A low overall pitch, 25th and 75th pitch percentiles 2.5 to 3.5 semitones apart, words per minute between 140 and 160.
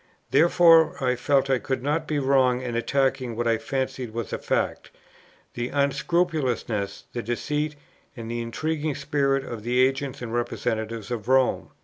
Yes: low, 130 Hz; average, 3.2 semitones; average, 155 wpm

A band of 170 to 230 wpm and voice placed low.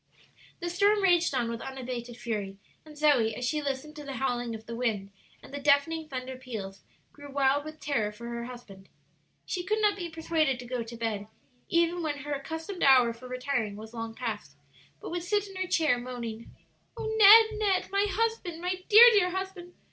No: average, 195 wpm; very high, 280 Hz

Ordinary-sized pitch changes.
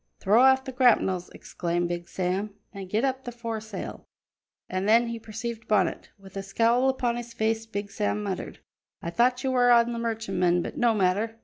Yes: average, 3.6 semitones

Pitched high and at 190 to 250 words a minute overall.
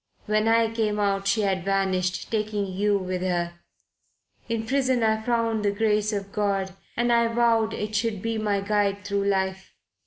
No: high, 210 Hz; average, 175 wpm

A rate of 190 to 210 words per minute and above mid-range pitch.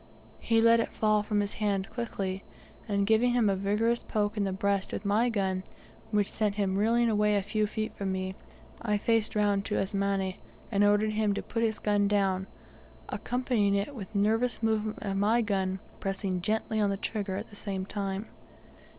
Yes: average, 195 wpm; high, 205 Hz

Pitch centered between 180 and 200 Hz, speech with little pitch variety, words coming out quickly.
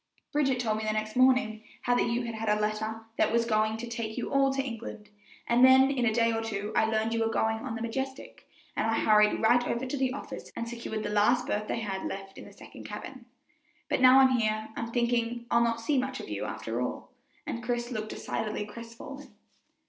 No: high, 230 Hz; narrow, 2.3 semitones; fast, 230 wpm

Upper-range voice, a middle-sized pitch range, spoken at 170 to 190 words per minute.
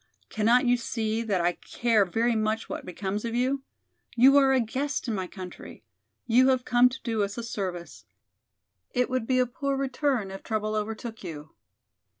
Yes: high, 230 Hz; average, 3.5 semitones; average, 180 wpm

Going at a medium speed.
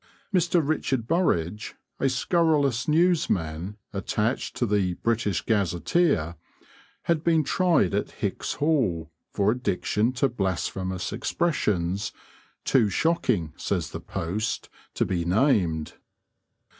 No: slow, 105 wpm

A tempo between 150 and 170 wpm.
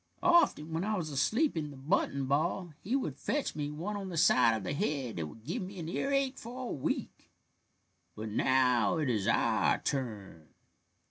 No: average, 190 wpm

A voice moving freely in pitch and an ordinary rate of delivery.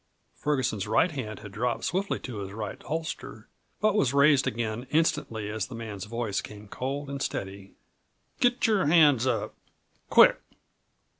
Yes: wide, 5.8 semitones; average, 150 wpm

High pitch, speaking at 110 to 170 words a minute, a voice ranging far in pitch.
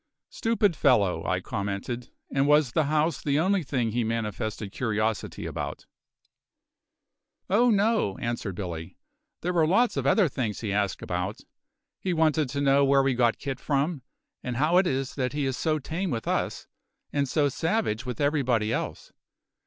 No: low, 135 Hz; average, 165 wpm; wide, 5.7 semitones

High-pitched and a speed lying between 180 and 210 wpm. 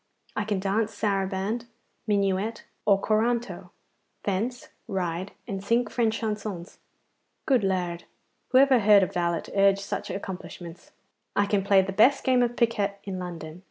No: high, 200 Hz; average, 145 wpm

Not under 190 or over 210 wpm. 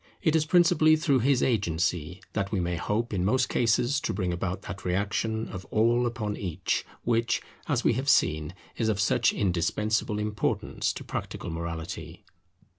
No: average, 165 wpm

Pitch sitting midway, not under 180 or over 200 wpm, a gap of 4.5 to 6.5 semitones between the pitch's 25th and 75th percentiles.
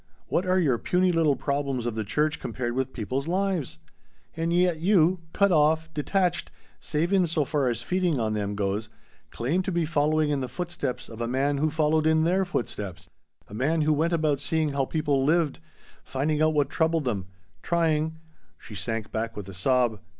Yes: medium, 150 Hz; average, 195 wpm; average, 4.9 semitones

